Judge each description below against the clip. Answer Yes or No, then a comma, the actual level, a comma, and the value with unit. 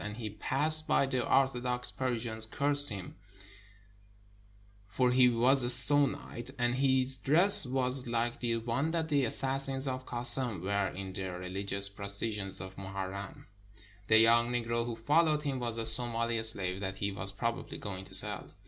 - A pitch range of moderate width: Yes, average, 4.5 semitones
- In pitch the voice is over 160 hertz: No, low, 120 Hz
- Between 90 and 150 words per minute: No, average, 165 wpm